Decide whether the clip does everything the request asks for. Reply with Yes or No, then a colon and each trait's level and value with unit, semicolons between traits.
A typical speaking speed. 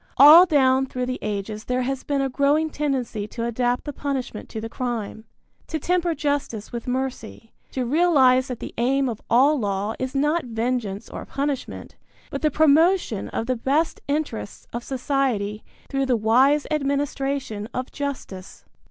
Yes: average, 160 wpm